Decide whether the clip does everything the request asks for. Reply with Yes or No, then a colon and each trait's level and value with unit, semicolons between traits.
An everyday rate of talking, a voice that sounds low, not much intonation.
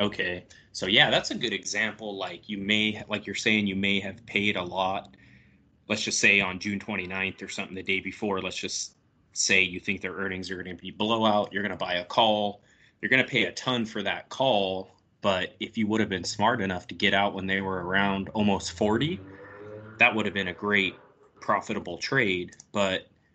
No: fast, 215 wpm; low, 100 Hz; narrow, 2.0 semitones